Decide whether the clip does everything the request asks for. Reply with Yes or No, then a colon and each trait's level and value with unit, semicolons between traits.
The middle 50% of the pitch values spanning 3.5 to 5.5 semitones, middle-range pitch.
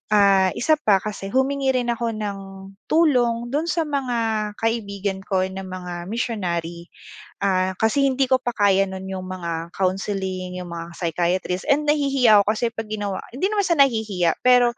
No: average, 5.1 semitones; high, 205 Hz